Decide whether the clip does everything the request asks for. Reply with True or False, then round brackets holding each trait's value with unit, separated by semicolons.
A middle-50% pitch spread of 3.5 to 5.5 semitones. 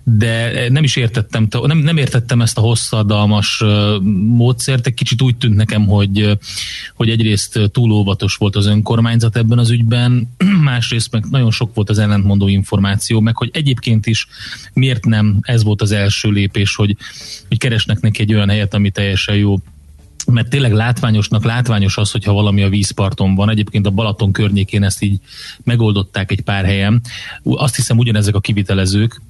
False (2.6 semitones)